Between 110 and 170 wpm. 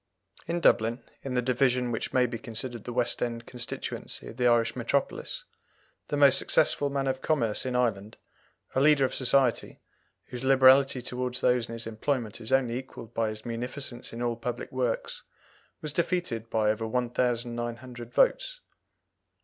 Yes: average, 160 wpm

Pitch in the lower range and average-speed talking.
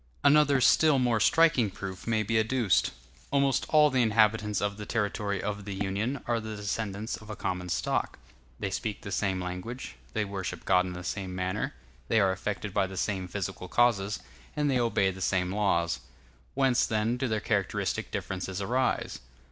Yes: low, 105 Hz; average, 180 wpm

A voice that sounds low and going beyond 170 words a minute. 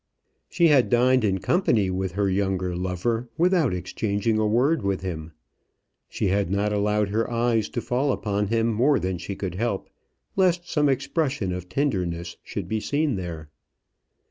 No: low, 105 Hz; average, 165 wpm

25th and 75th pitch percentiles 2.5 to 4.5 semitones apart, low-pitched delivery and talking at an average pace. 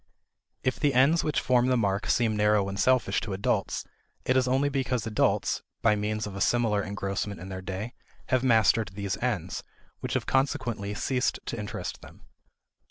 Yes: average, 4.2 semitones; low, 110 Hz; average, 175 wpm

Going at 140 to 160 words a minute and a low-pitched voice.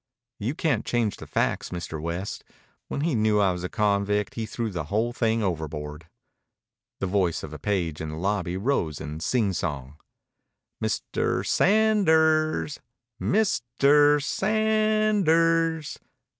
Yes: average, 155 wpm; low, 110 Hz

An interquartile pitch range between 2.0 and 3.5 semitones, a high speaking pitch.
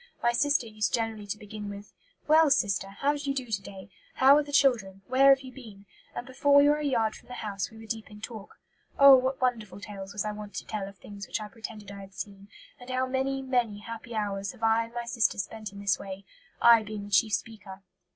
No: average, 4.2 semitones; high, 220 Hz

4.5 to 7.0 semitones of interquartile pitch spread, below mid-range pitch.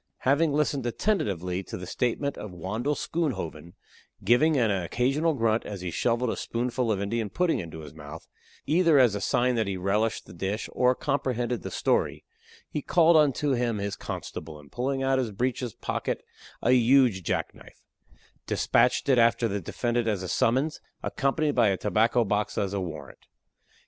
Yes: wide, 5.4 semitones; low, 115 Hz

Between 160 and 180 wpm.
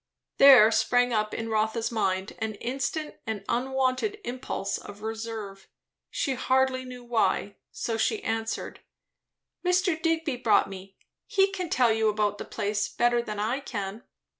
No: average, 145 wpm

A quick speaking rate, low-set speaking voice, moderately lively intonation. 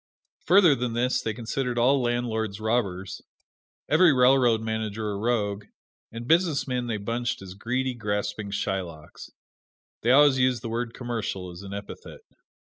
No: average, 140 wpm; low, 115 Hz; average, 3.4 semitones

